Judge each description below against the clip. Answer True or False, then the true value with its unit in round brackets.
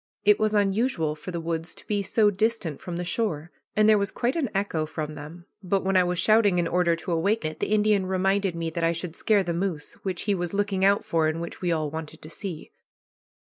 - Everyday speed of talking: False (240 wpm)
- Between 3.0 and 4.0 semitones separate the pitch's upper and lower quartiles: True (3.5 semitones)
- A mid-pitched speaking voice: True (180 Hz)